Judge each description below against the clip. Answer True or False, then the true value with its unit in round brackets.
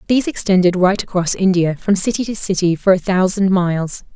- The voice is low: False (190 Hz)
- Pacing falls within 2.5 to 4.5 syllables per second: False (5.7 syllables/s)